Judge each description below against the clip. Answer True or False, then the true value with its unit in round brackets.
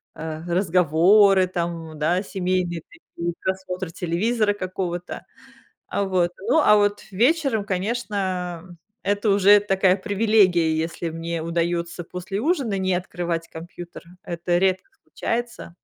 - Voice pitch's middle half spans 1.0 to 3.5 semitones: True (2.9 semitones)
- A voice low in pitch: False (185 Hz)